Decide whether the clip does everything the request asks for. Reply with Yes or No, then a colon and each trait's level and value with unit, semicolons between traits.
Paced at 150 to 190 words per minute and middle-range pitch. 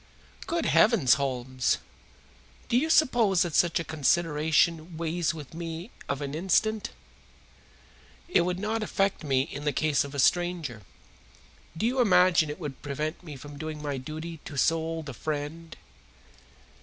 Yes: average, 155 wpm; medium, 160 Hz